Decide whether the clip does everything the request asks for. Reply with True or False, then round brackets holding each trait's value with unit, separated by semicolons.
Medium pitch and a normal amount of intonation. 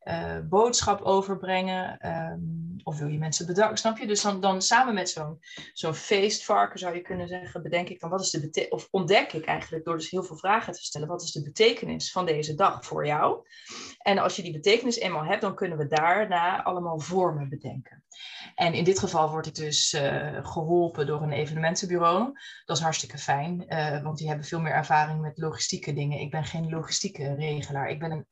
True (165 Hz; 3.6 semitones)